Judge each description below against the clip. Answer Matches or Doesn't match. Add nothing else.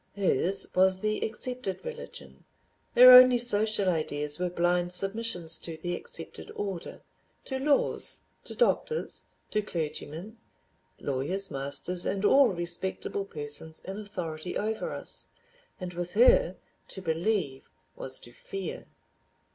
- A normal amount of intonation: Matches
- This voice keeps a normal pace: Doesn't match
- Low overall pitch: Doesn't match